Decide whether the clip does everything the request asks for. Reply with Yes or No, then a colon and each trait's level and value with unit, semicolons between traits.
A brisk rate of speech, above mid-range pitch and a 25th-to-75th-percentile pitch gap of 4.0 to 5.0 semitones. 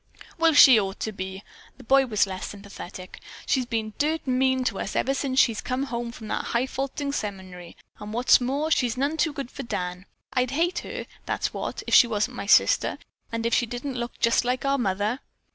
Yes: fast, 210 wpm; high, 240 Hz; average, 4.3 semitones